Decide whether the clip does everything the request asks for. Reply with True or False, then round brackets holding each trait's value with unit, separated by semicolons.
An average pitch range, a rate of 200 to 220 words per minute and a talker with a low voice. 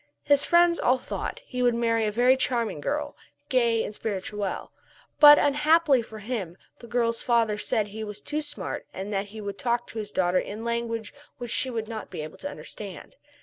False (3.6 semitones; 205 wpm; 230 Hz)